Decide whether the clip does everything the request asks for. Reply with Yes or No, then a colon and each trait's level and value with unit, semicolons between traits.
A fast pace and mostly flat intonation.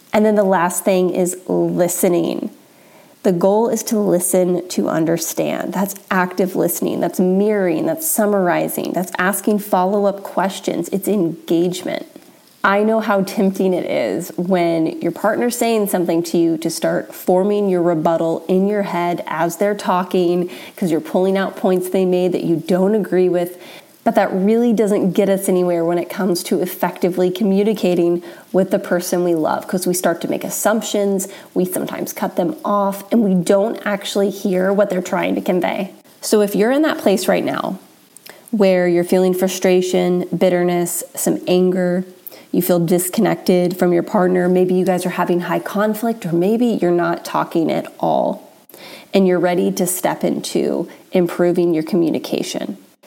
No: average, 165 wpm; narrow, 2.2 semitones